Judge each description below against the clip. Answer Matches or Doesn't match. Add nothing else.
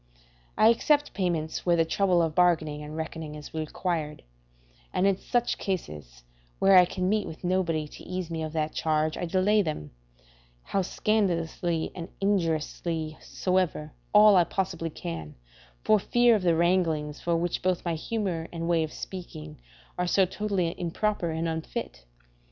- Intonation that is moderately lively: Matches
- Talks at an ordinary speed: Matches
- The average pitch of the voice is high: Doesn't match